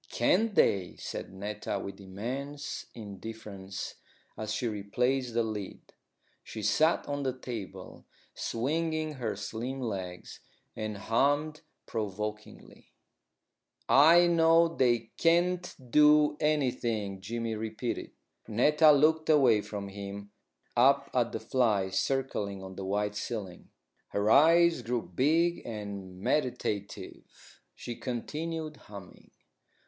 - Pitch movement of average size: No, wide, 6.5 semitones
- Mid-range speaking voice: No, low, 120 Hz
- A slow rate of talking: Yes, slow, 110 wpm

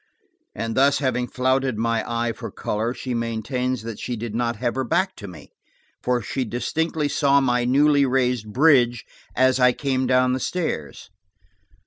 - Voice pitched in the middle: No, low, 125 Hz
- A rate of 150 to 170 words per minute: Yes, average, 165 wpm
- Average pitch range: No, narrow, 2.3 semitones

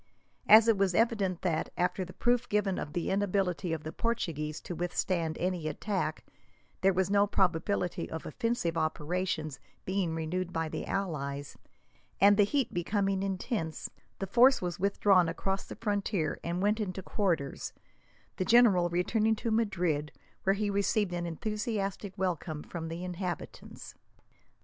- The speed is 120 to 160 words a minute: Yes, average, 150 wpm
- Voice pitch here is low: No, medium, 185 Hz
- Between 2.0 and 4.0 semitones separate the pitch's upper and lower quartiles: Yes, average, 3.3 semitones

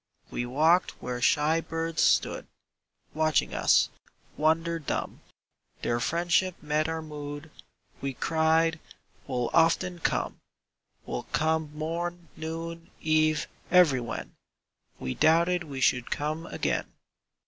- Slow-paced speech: Yes, slow, 110 wpm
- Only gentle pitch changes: Yes, narrow, 2.0 semitones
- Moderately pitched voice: Yes, medium, 160 Hz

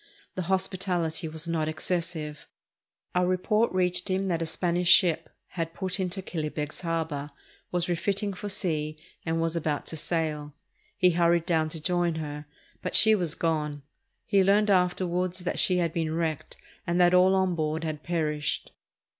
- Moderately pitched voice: Yes, medium, 170 Hz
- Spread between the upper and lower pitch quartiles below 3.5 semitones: Yes, narrow, 2.5 semitones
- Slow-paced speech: No, average, 165 wpm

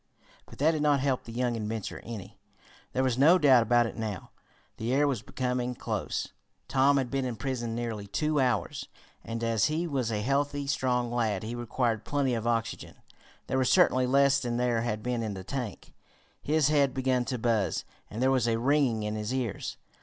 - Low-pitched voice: Yes, low, 125 Hz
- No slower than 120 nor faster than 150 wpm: No, average, 195 wpm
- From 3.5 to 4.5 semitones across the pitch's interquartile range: No, average, 3.1 semitones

